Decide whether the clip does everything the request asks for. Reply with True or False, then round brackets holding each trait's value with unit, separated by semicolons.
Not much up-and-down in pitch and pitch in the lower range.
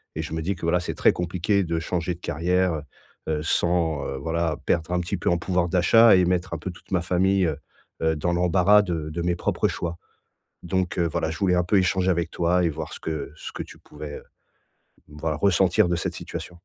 True (2.0 semitones; 85 Hz)